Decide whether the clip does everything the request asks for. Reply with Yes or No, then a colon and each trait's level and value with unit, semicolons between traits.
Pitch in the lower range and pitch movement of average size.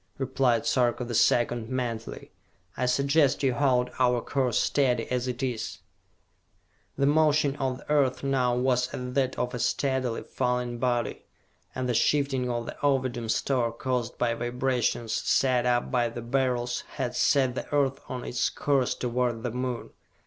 No: low, 125 Hz; narrow, 1.7 semitones